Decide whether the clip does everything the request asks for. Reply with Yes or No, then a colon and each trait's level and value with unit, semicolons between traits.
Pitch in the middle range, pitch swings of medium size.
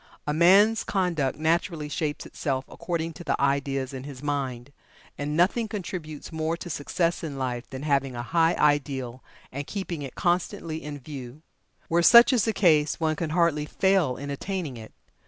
Yes: medium, 150 Hz; average, 3.8 semitones